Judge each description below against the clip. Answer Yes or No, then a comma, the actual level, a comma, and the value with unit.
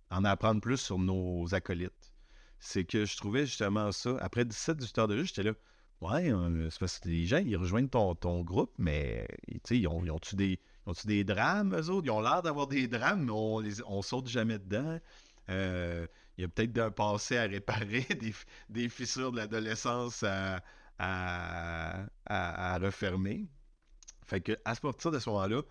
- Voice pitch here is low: Yes, low, 105 Hz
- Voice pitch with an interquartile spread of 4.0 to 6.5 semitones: Yes, average, 4.4 semitones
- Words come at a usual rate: Yes, average, 195 wpm